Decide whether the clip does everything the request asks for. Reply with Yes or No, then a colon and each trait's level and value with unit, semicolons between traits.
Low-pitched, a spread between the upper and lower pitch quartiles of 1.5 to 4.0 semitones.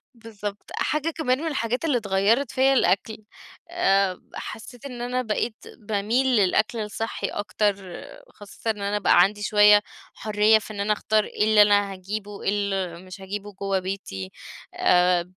No: high, 210 Hz; narrow, 2.4 semitones